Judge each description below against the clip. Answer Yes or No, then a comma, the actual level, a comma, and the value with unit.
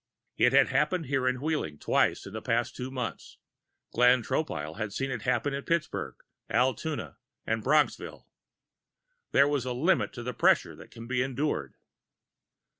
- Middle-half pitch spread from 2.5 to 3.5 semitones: Yes, average, 3.1 semitones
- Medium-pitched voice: No, low, 125 Hz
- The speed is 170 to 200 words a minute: No, average, 160 wpm